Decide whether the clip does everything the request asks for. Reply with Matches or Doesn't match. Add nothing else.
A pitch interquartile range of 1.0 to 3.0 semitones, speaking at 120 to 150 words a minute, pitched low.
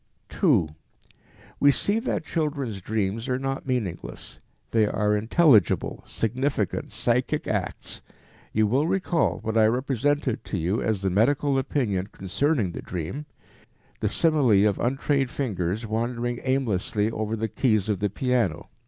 Doesn't match